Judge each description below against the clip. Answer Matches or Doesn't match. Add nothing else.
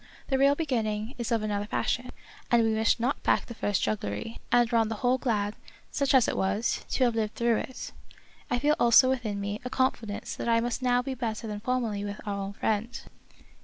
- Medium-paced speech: Doesn't match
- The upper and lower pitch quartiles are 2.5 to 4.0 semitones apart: Matches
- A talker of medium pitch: Doesn't match